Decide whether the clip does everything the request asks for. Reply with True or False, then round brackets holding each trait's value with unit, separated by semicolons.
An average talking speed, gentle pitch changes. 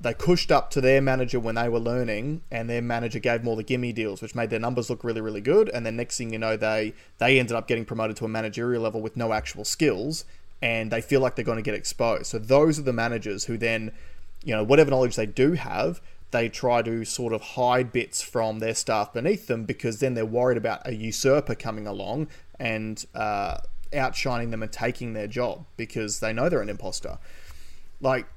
False (225 wpm; 2.1 semitones)